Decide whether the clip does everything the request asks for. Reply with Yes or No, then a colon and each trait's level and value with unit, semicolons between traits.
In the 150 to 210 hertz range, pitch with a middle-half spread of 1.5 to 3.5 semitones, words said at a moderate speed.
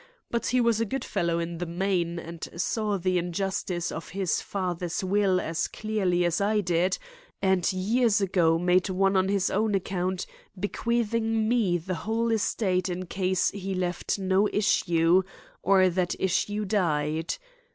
Yes: high, 190 Hz; average, 2.7 semitones; average, 155 wpm